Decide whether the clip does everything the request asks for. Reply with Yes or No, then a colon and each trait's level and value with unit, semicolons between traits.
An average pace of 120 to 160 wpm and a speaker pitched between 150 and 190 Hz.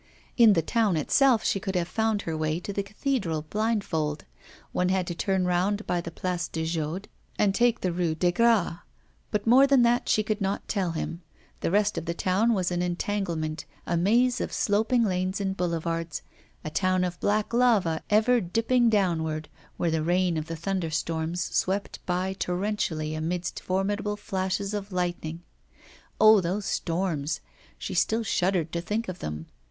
No: average, 175 wpm; medium, 185 Hz